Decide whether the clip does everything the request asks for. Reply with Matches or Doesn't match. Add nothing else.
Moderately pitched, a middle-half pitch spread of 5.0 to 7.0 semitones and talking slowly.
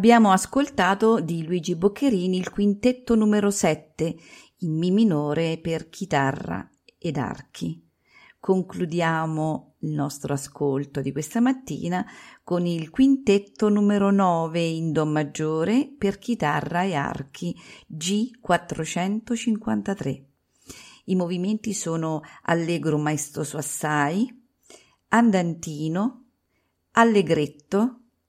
Matches